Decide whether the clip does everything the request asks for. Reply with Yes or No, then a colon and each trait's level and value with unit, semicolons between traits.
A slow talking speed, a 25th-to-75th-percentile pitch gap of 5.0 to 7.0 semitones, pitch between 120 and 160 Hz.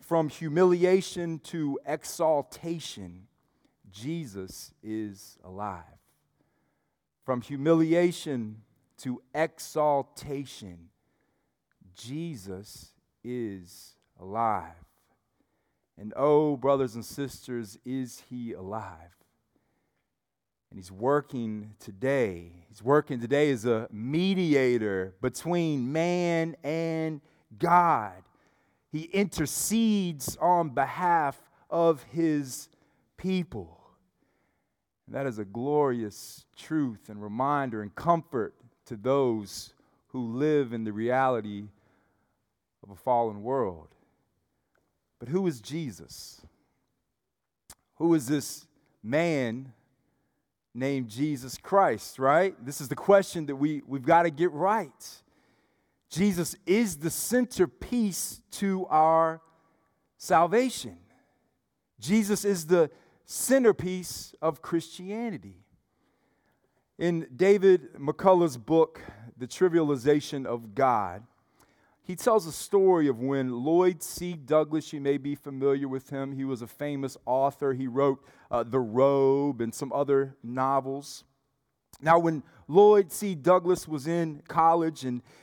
Yes: slow, 105 wpm; wide, 5.4 semitones; medium, 140 Hz